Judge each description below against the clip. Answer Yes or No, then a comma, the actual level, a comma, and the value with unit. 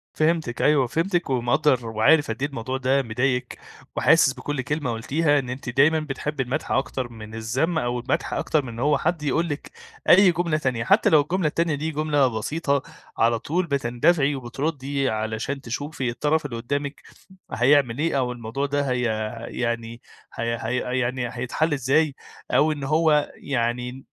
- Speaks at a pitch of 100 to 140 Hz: Yes, low, 135 Hz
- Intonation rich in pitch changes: No, average, 3.7 semitones